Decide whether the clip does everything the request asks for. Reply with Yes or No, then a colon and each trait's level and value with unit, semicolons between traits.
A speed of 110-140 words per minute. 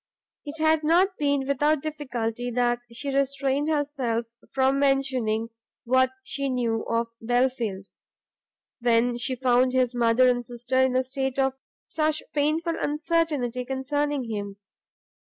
Yes: slow, 135 wpm